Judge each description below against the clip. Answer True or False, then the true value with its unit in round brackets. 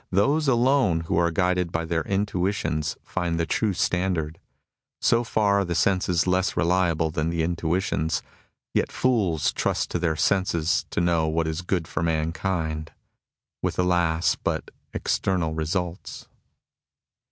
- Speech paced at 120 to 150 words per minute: True (140 wpm)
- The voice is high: False (85 Hz)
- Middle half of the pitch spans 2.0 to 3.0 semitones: True (2.6 semitones)